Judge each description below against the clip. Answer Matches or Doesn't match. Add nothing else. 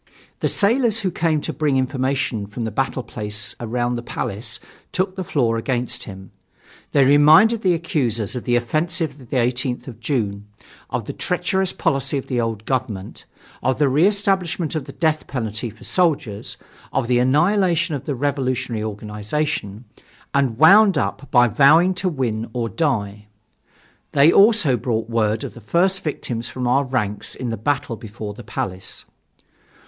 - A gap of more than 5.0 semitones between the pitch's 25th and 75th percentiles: Matches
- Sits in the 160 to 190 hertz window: Doesn't match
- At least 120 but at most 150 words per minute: Doesn't match